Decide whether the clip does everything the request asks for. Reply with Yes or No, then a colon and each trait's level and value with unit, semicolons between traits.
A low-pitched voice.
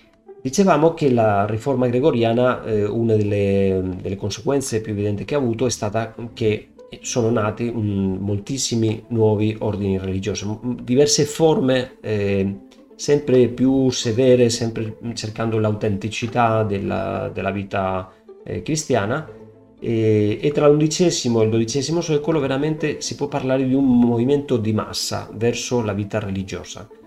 Yes: low, 115 Hz